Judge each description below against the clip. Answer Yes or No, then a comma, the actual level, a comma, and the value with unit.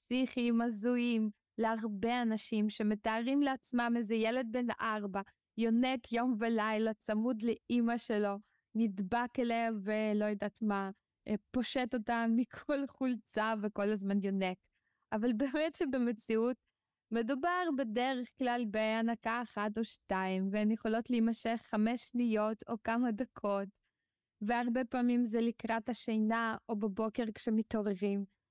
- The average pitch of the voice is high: Yes, high, 230 Hz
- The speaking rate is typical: Yes, average, 110 wpm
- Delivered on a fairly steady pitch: Yes, narrow, 2.1 semitones